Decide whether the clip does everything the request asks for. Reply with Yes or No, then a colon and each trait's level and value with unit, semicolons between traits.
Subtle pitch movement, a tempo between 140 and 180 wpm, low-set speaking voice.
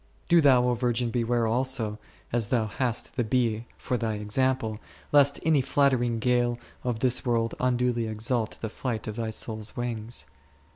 Yes: narrow, 2.2 semitones; average, 160 wpm; low, 120 Hz